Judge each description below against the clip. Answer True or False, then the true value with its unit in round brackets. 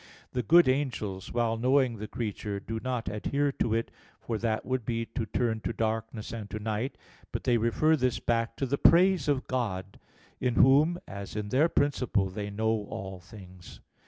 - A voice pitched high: False (115 Hz)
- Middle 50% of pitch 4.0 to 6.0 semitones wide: False (3.5 semitones)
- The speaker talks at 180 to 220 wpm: True (185 wpm)